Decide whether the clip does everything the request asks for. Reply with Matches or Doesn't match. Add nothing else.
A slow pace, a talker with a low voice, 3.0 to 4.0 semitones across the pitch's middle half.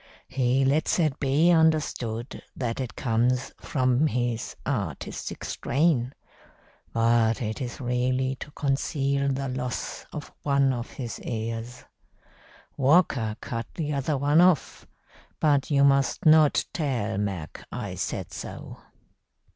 Matches